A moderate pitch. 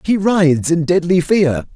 Yes: medium, 165 Hz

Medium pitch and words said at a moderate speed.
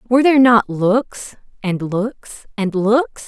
No: high, 220 Hz; average, 145 wpm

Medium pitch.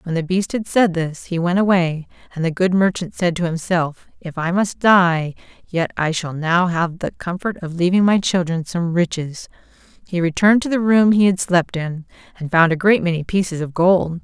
Yes: medium, 175 Hz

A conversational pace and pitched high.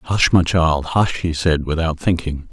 No: average, 190 wpm; very low, 80 Hz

